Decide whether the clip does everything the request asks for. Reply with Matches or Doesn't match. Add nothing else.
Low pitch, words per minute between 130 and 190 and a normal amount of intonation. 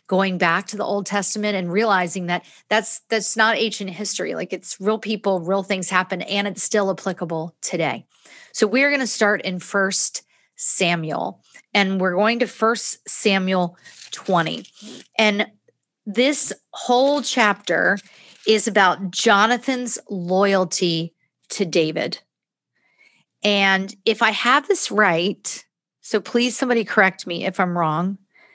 Doesn't match